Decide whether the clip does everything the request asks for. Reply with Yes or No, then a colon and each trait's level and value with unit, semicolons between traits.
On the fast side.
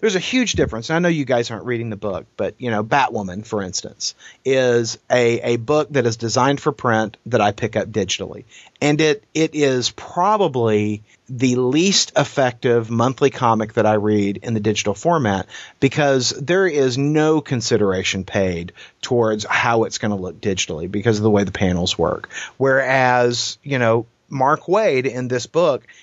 No: average, 180 wpm